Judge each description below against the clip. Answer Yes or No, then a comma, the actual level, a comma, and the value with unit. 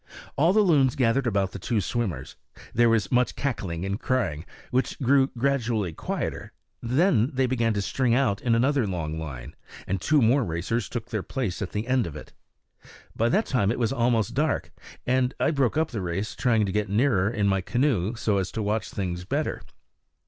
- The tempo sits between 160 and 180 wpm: No, average, 195 wpm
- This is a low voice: Yes, low, 115 Hz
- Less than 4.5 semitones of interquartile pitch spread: No, average, 4.8 semitones